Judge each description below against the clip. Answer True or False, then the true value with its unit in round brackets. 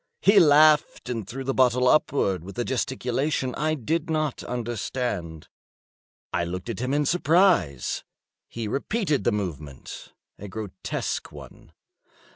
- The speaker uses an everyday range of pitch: False (6.7 semitones)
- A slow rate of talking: True (125 wpm)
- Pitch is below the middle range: True (125 Hz)